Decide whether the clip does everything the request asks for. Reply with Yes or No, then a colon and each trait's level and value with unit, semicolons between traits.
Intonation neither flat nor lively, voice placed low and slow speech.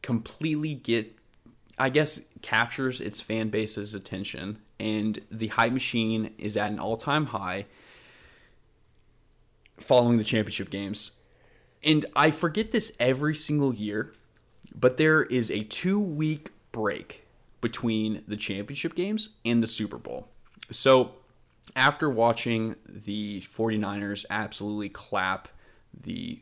Yes: average, 4.7 semitones; low, 115 Hz; slow, 115 wpm